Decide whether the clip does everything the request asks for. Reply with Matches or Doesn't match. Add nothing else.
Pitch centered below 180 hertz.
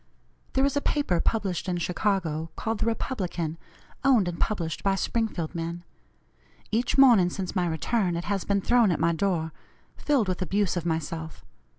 Doesn't match